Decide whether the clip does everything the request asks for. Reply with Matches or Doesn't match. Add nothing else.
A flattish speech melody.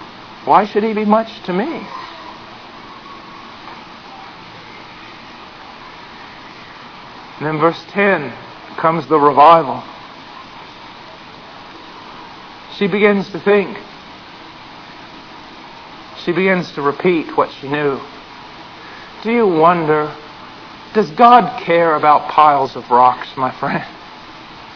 Doesn't match